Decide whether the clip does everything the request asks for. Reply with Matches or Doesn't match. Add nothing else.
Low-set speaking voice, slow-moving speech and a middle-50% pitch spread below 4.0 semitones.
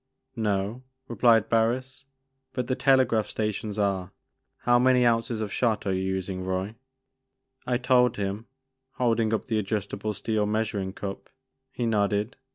Doesn't match